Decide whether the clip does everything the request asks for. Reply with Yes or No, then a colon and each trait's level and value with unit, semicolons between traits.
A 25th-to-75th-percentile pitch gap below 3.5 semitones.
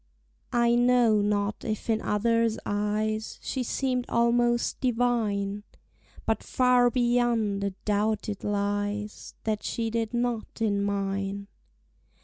Yes: average, 2.7 semitones